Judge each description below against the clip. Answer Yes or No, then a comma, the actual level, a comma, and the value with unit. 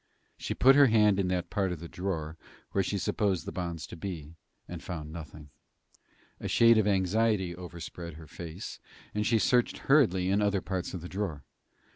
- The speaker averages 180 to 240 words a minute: Yes, average, 185 wpm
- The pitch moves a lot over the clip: No, average, 3.6 semitones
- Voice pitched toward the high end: No, very low, 95 Hz